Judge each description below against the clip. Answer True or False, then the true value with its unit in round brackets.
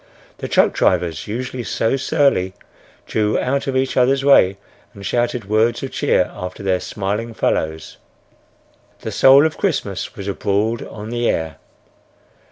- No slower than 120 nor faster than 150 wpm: True (145 wpm)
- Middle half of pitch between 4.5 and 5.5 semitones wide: True (5.0 semitones)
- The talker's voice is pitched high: False (110 Hz)